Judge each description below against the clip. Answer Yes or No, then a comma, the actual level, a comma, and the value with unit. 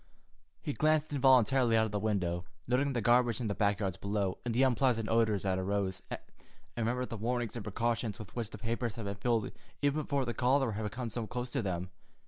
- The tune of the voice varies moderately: Yes, average, 3.6 semitones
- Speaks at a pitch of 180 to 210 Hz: No, low, 115 Hz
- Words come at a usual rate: No, fast, 215 wpm